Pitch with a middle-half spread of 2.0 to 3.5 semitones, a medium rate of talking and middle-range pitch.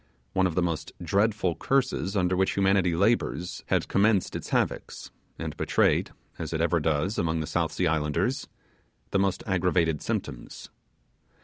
No: average, 3.0 semitones; average, 150 wpm; very low, 90 Hz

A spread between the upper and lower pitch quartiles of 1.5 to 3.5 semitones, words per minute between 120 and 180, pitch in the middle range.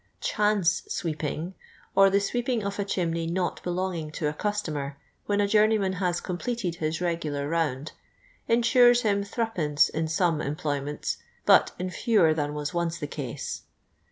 No: average, 4.8 semitones; average, 160 wpm; medium, 175 Hz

